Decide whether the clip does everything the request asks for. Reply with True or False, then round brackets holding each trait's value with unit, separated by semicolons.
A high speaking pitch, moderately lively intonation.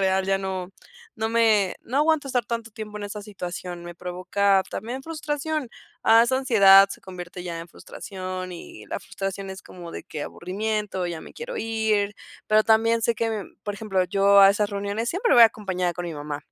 True (200 Hz; 3.5 semitones)